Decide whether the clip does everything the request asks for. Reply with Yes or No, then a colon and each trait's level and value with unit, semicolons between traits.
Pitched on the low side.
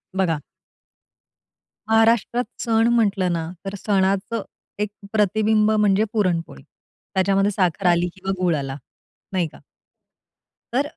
No: high, 195 Hz